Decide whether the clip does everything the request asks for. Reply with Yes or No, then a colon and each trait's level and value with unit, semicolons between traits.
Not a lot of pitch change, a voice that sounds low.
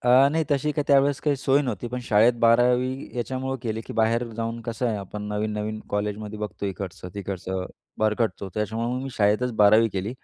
No: average, 3.2 semitones; low, 115 Hz